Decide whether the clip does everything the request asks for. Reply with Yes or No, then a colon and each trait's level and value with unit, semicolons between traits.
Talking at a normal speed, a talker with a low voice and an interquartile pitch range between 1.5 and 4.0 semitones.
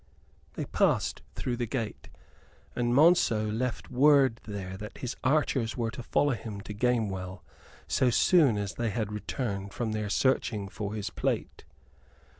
Yes: average, 150 wpm; low, 115 Hz; average, 3.5 semitones